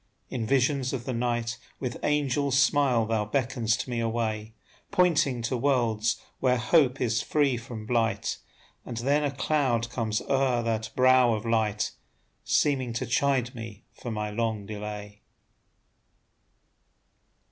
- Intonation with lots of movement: No, average, 3.0 semitones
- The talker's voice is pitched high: No, low, 120 Hz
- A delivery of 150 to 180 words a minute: No, slow, 135 wpm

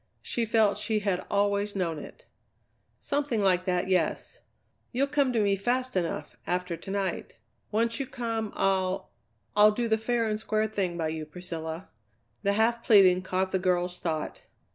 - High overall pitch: Yes, high, 200 Hz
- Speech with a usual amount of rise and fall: Yes, average, 3.7 semitones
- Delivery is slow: No, average, 165 wpm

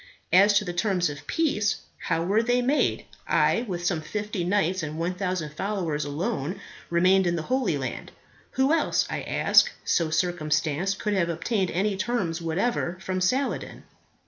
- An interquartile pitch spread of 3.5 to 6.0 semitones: Yes, average, 3.8 semitones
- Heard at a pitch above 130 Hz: Yes, medium, 185 Hz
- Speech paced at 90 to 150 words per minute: No, average, 160 wpm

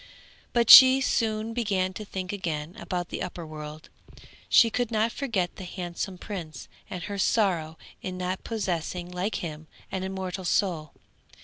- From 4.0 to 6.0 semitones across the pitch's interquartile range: No, average, 3.6 semitones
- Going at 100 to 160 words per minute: Yes, average, 150 wpm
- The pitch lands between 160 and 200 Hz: Yes, medium, 185 Hz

